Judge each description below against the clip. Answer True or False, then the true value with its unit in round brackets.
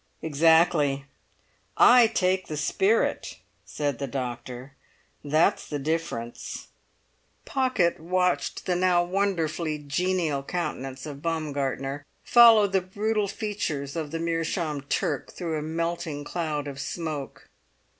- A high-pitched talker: False (160 Hz)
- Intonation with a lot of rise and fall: False (4.2 semitones)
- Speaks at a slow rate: True (115 wpm)